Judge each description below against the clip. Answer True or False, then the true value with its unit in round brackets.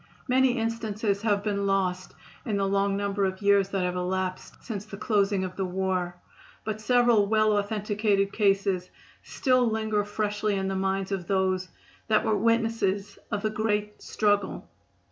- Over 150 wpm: True (160 wpm)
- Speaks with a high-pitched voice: True (200 Hz)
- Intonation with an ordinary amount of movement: False (1.9 semitones)